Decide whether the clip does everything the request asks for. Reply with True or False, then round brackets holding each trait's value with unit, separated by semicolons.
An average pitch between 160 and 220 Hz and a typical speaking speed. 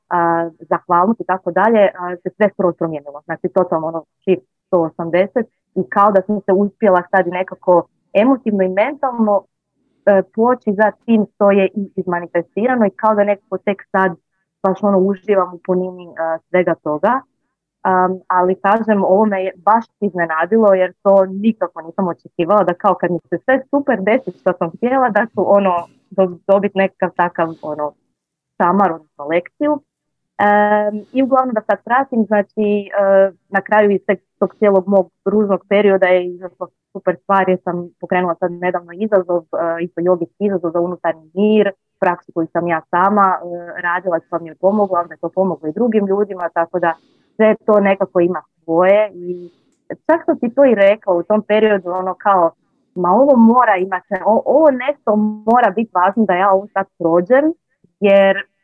False (190 Hz; 170 wpm)